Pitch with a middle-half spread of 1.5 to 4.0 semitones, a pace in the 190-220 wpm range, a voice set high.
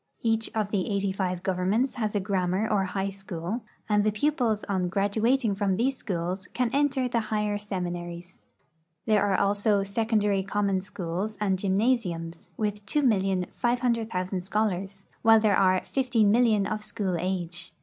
No: average, 2.8 semitones; average, 145 wpm; high, 205 Hz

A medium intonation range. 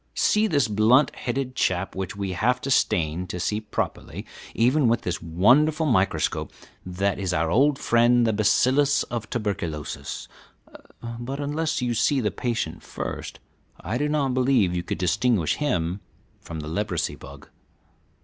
No: wide, 6.3 semitones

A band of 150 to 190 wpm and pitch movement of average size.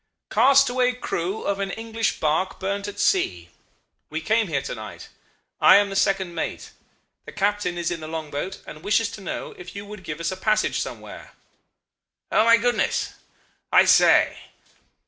Yes: average, 170 wpm; average, 4.2 semitones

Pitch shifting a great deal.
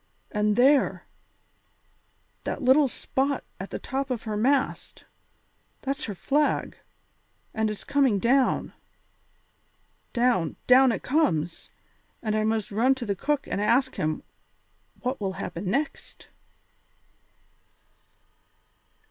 No: average, 4.5 semitones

